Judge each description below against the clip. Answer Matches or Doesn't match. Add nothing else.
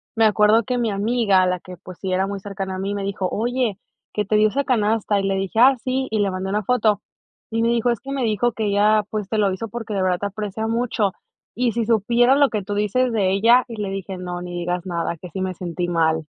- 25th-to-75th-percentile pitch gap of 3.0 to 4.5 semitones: Matches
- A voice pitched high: Matches